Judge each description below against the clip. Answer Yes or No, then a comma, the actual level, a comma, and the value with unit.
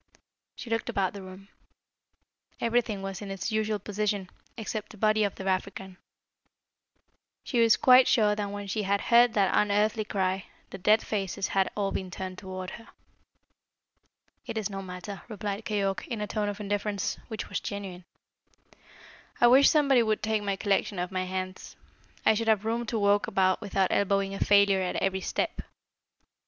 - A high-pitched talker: Yes, high, 205 Hz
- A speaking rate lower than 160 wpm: No, average, 170 wpm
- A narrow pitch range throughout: Yes, narrow, 2.0 semitones